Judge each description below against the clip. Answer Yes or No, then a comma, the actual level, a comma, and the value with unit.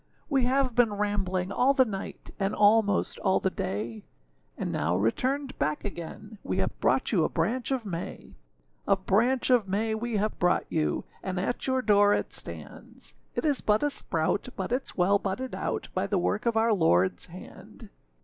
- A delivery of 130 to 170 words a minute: No, average, 185 wpm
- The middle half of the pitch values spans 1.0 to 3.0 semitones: No, average, 4.7 semitones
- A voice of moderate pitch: No, high, 205 Hz